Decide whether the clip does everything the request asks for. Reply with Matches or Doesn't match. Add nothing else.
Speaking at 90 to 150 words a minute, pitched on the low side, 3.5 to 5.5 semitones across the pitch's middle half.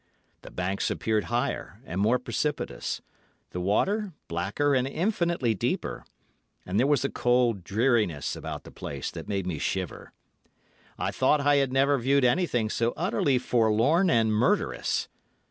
Matches